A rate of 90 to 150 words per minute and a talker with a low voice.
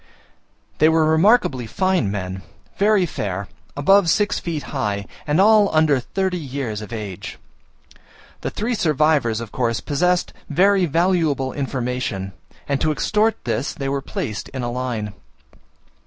No: average, 140 wpm; medium, 145 Hz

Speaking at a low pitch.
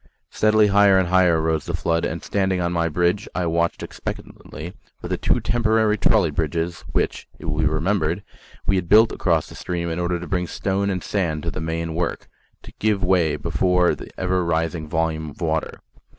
Yes: very low, 85 Hz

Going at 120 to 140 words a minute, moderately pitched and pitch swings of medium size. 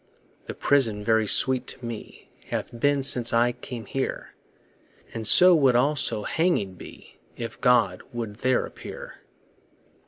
No: slow, 135 wpm; low, 120 Hz; average, 3.1 semitones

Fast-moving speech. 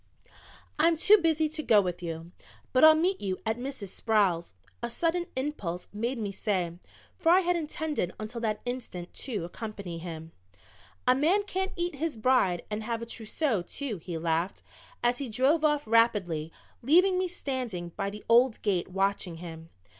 No: average, 170 wpm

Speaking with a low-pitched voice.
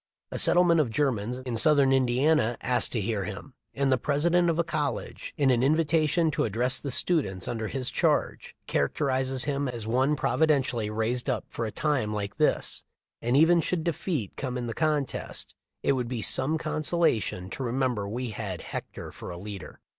Yes: low, 130 Hz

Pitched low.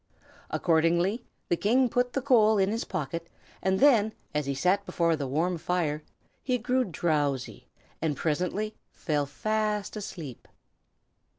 No: medium, 180 Hz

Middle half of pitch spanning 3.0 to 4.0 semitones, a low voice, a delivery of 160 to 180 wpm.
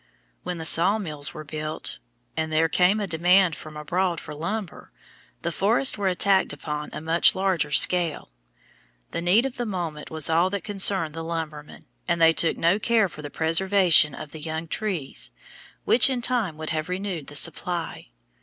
No: average, 3.6 semitones; medium, 170 Hz; average, 175 wpm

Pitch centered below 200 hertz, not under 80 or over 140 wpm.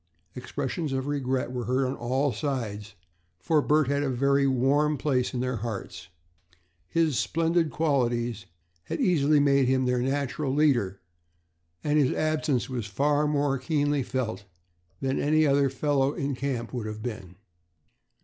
No: low, 135 Hz; average, 160 wpm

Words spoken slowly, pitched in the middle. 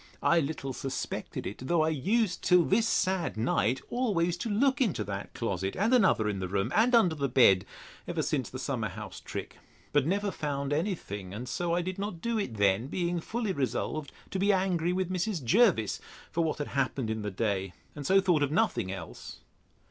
No: average, 200 wpm; medium, 160 Hz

